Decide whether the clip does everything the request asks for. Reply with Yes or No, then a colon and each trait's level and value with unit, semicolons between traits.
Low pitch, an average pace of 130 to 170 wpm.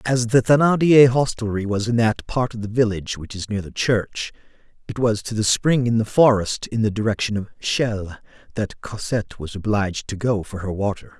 No: low, 110 Hz; fast, 205 wpm